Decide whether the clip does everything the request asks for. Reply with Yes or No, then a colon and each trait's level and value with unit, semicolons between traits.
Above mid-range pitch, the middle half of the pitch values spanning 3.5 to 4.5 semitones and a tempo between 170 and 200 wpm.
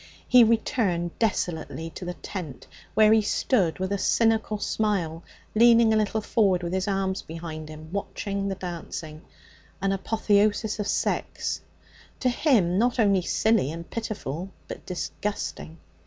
No: high, 195 Hz; average, 4.1 semitones; average, 140 wpm